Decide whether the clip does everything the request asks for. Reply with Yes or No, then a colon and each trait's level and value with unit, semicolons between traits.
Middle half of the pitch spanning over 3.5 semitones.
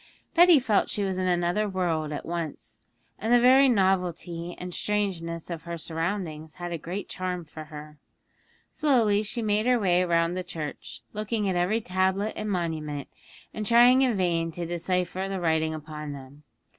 Yes: average, 3.9 semitones